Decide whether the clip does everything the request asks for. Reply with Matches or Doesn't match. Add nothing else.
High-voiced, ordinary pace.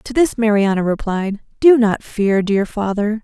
Matches